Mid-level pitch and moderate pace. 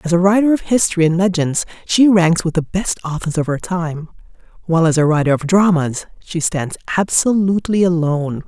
Yes: medium, 175 Hz; average, 185 wpm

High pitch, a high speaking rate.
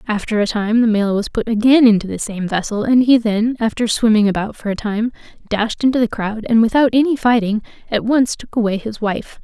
Yes: high, 225 Hz; fast, 225 wpm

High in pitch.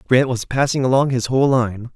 No: low, 130 Hz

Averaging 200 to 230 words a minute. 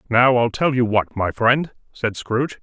Yes: fast, 205 wpm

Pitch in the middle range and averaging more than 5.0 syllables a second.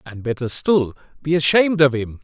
Yes: medium, 145 Hz; 5.4 syllables/s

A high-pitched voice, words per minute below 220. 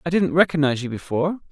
No: medium, 155 Hz; average, 200 wpm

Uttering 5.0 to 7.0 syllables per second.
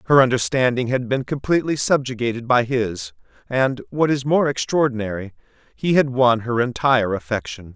Yes: 5.4 syllables/s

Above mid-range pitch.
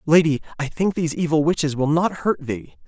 No: medium, 155 Hz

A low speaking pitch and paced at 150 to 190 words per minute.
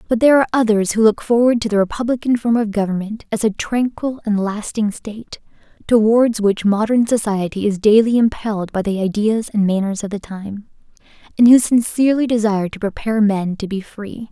No: high, 215 Hz; average, 185 wpm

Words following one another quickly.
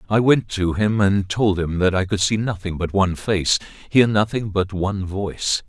Yes: fast, 210 wpm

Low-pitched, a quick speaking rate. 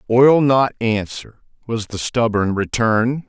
No: low, 115 Hz; slow, 130 wpm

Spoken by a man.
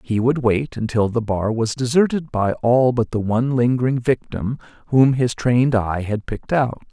Yes: male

